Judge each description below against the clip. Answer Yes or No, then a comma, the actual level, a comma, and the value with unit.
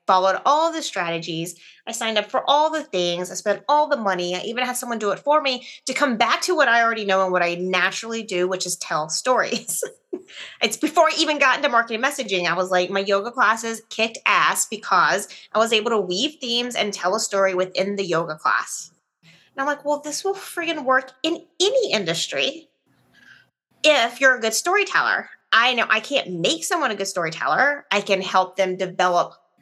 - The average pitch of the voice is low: No, high, 225 Hz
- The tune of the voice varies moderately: No, wide, 7.4 semitones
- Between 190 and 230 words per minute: Yes, fast, 205 wpm